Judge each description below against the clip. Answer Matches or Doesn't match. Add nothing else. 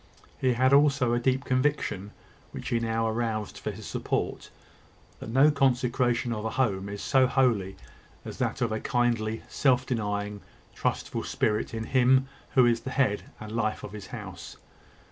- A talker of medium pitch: Doesn't match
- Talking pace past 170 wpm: Doesn't match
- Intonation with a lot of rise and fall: Doesn't match